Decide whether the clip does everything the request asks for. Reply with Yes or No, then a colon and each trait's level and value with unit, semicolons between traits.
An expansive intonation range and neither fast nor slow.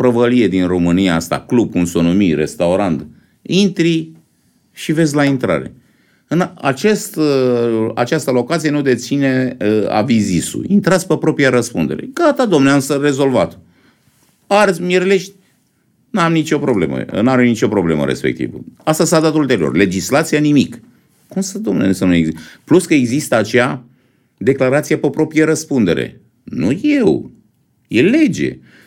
Yes: wide, 5.9 semitones; average, 135 wpm